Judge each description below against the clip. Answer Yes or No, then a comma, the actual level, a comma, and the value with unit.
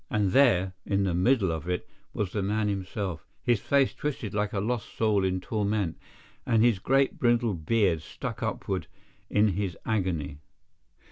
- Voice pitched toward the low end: Yes, low, 105 Hz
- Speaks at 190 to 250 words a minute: No, average, 155 wpm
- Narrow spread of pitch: No, average, 3.6 semitones